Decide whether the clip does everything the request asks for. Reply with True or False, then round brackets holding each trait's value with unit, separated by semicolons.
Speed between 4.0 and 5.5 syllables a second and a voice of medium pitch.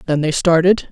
True (5.3 syllables/s; 165 Hz)